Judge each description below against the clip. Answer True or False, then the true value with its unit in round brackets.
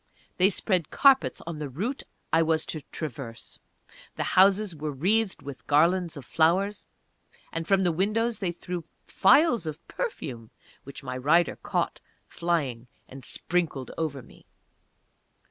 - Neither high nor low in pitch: True (165 Hz)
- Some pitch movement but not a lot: True (5.0 semitones)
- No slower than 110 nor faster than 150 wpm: True (140 wpm)